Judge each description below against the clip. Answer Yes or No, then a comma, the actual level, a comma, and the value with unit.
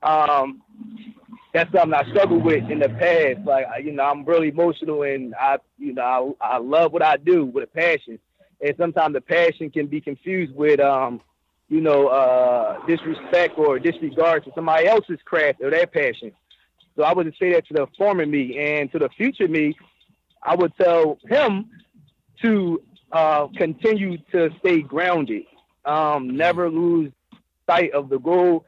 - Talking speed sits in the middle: Yes, average, 170 wpm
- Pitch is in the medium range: Yes, medium, 165 Hz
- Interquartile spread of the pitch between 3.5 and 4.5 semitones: Yes, average, 4.2 semitones